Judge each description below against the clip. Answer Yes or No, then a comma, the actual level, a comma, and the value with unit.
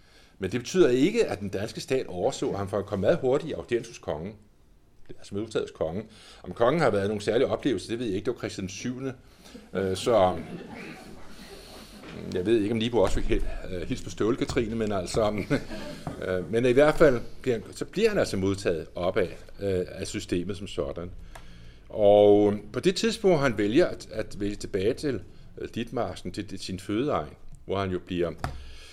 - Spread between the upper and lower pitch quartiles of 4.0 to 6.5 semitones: No, average, 3.4 semitones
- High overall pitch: No, low, 100 Hz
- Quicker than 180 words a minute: No, average, 175 wpm